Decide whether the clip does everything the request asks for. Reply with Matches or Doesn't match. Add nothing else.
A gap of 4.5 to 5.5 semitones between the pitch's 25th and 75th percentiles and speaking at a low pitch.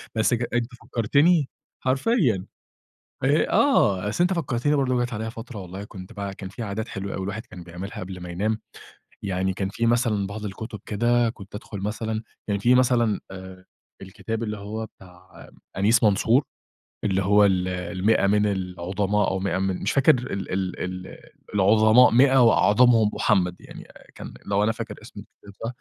Doesn't match